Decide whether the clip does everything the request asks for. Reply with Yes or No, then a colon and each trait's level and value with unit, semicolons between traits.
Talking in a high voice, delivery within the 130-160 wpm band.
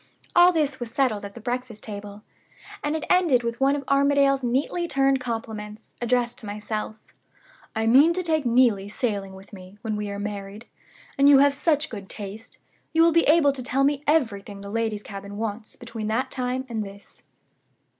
No: high, 235 Hz; average, 185 wpm